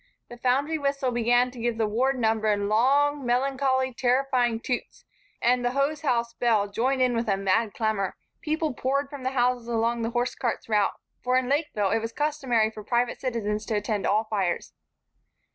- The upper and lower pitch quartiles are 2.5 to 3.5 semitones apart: Yes, average, 3.0 semitones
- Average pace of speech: Yes, average, 180 wpm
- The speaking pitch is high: Yes, high, 240 Hz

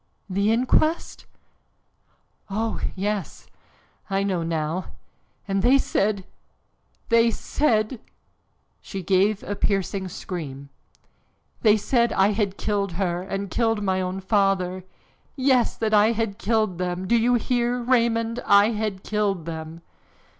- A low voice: No, high, 205 Hz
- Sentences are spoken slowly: Yes, slow, 125 wpm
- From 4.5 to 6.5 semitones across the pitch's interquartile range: No, average, 3.3 semitones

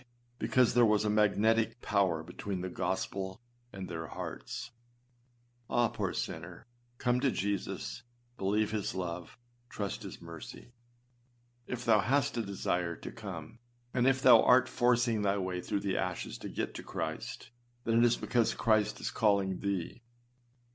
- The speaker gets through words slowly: No, average, 150 wpm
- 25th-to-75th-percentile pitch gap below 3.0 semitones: No, average, 3.8 semitones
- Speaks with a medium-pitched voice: No, low, 105 Hz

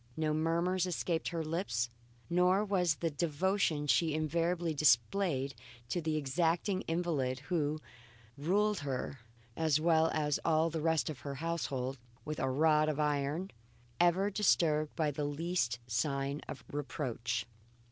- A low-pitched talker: No, medium, 155 Hz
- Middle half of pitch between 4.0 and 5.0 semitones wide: No, average, 3.2 semitones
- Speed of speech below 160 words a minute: Yes, slow, 135 wpm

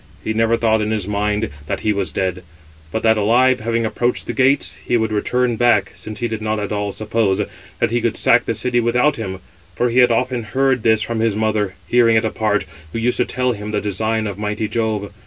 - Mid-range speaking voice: No, low, 110 Hz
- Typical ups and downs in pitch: No, narrow, 2.2 semitones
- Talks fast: Yes, fast, 230 wpm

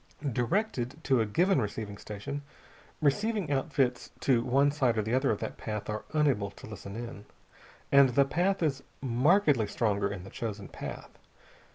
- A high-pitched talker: No, low, 125 Hz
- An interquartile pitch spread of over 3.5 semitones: Yes, average, 5.0 semitones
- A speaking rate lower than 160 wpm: No, average, 165 wpm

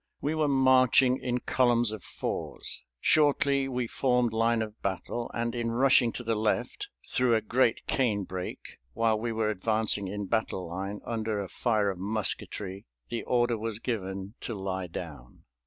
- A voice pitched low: Yes, low, 115 Hz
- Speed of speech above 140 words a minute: Yes, average, 165 wpm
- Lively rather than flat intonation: No, average, 3.4 semitones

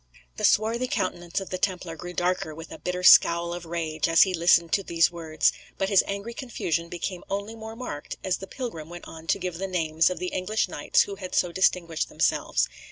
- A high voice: No, medium, 180 Hz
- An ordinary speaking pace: No, fast, 215 wpm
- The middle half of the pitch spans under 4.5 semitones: Yes, narrow, 2.6 semitones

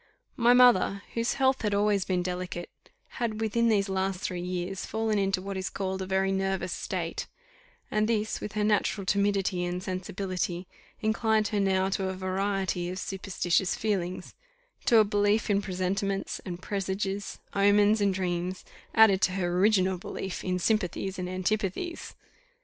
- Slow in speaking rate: No, average, 155 wpm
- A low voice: No, high, 195 Hz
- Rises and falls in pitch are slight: Yes, narrow, 2.1 semitones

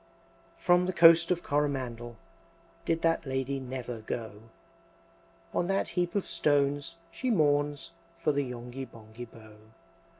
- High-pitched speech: No, medium, 140 Hz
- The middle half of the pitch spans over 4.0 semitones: Yes, wide, 5.4 semitones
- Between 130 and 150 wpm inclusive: Yes, slow, 135 wpm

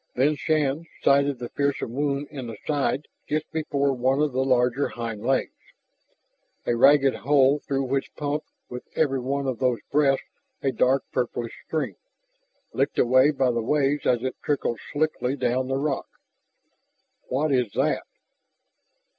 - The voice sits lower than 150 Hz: Yes, low, 135 Hz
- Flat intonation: Yes, narrow, 2.3 semitones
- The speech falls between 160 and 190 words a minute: No, average, 150 wpm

